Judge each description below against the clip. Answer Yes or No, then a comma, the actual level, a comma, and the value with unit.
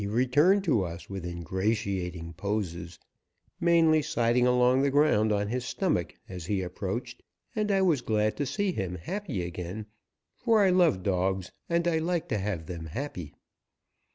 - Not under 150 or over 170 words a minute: Yes, average, 160 wpm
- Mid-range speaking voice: No, low, 110 Hz